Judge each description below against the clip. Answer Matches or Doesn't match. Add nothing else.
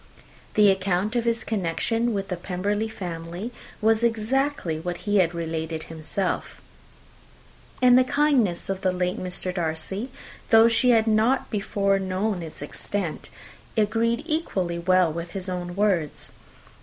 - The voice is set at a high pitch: Matches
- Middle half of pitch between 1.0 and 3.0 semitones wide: Doesn't match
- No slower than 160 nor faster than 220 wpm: Doesn't match